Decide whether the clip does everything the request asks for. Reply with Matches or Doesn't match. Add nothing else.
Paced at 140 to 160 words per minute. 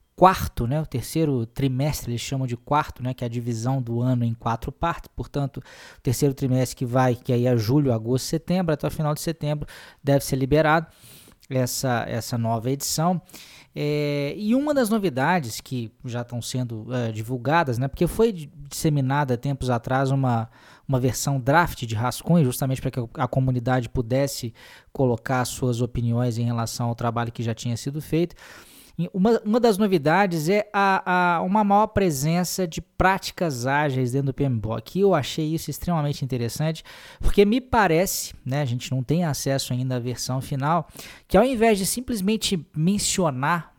Doesn't match